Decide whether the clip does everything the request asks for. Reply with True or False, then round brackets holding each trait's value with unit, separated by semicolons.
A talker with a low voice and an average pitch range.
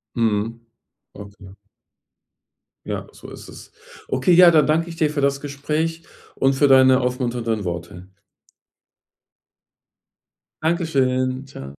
True (130 Hz; 4.9 semitones)